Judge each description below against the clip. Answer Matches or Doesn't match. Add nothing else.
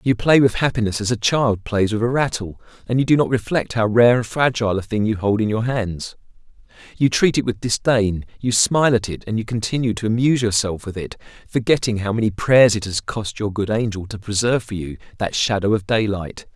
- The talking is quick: Matches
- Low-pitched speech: Matches